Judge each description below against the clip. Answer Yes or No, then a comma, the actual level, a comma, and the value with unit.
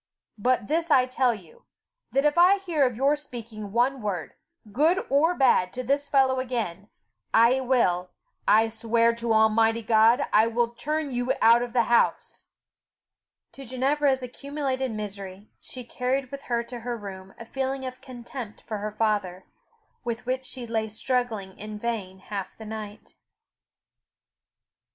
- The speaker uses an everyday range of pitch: Yes, average, 3.4 semitones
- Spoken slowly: No, average, 155 wpm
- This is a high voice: Yes, high, 235 Hz